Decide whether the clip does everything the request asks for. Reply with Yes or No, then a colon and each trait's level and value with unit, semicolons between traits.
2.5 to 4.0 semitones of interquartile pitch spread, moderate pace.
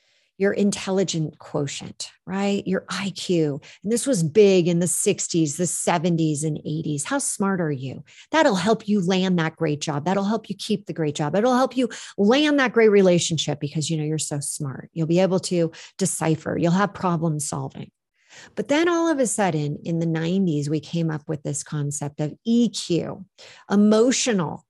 No: average, 4.5 semitones; average, 180 wpm